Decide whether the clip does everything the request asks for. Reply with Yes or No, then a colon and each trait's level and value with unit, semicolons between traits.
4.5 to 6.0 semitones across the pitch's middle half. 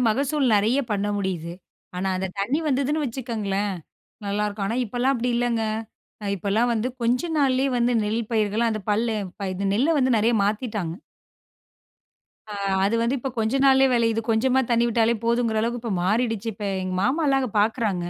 No: average, 3.4 semitones